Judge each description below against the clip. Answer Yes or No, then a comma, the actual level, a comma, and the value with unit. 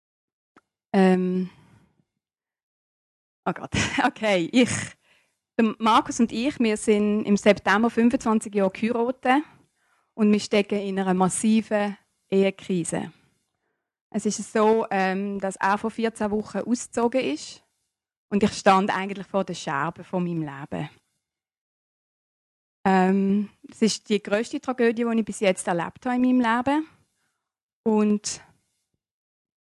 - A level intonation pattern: No, average, 3.3 semitones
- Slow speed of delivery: Yes, slow, 120 wpm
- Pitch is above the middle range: Yes, high, 210 Hz